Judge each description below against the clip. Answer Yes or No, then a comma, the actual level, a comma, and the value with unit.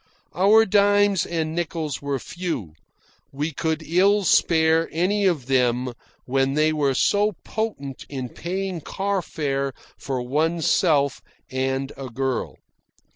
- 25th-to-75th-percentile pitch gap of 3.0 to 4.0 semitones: No, average, 5.3 semitones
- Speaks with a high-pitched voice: No, medium, 155 Hz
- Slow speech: Yes, slow, 125 wpm